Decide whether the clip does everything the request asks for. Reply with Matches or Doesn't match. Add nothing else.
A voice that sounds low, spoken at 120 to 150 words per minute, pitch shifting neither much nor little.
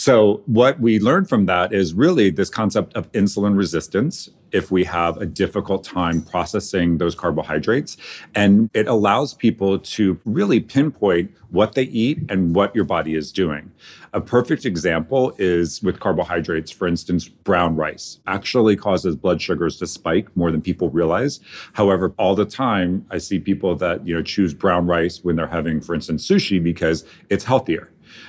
Doesn't match